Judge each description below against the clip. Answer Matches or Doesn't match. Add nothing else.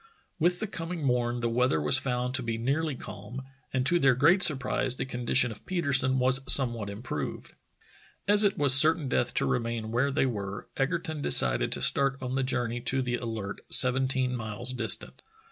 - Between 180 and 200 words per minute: Matches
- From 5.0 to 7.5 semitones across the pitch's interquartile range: Doesn't match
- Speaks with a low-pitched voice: Matches